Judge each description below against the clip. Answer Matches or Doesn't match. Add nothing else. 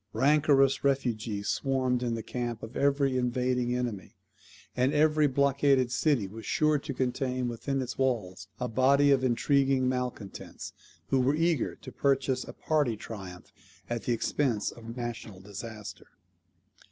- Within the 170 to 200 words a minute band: Doesn't match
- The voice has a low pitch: Matches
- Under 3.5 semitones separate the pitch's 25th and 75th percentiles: Matches